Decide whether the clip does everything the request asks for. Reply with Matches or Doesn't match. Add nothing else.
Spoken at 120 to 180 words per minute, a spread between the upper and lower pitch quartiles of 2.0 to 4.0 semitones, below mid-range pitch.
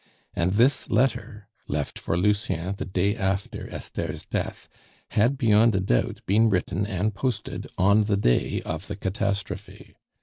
Matches